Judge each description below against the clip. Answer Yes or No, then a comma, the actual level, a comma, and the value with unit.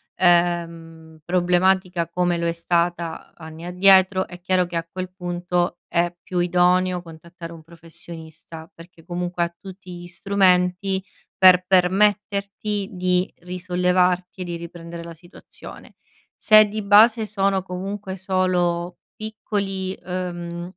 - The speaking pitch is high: No, medium, 180 Hz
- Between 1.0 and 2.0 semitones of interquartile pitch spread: Yes, narrow, 1.6 semitones